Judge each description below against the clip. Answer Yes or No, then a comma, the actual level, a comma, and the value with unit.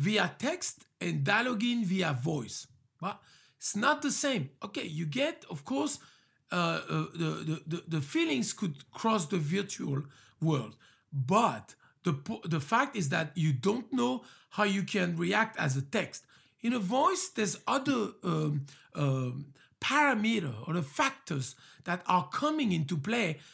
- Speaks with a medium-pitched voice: Yes, medium, 180 Hz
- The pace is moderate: Yes, average, 150 wpm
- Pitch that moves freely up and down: Yes, wide, 7.1 semitones